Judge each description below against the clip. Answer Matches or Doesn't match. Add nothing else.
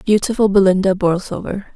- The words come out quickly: Doesn't match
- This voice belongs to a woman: Matches